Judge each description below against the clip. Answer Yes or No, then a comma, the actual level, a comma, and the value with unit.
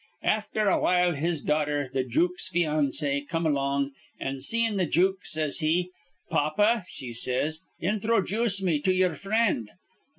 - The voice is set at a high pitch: No, medium, 165 Hz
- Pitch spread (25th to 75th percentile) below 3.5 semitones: No, average, 5.0 semitones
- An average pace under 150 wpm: Yes, slow, 135 wpm